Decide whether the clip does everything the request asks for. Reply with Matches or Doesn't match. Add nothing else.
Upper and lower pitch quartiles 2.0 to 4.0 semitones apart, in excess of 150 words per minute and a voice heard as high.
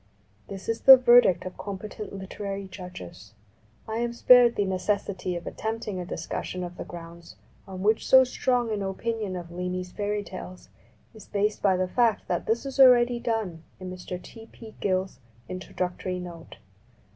Matches